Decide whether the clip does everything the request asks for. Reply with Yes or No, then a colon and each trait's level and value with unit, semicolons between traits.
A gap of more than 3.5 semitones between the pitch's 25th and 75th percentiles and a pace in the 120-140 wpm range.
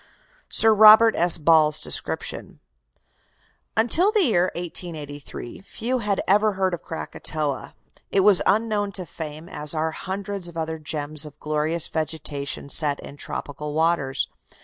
Yes: average, 4.9 semitones; slow, 135 wpm